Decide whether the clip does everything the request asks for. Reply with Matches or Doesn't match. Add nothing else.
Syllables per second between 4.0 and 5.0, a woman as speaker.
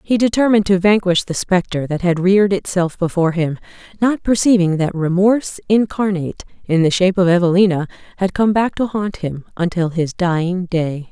Doesn't match